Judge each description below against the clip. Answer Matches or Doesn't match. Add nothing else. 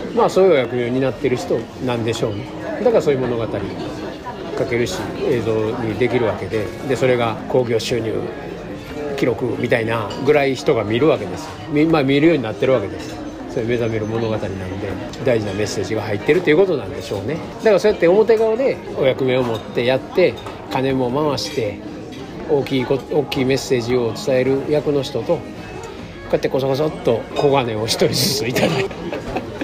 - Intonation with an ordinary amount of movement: Matches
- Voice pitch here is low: Matches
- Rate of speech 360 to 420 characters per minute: Matches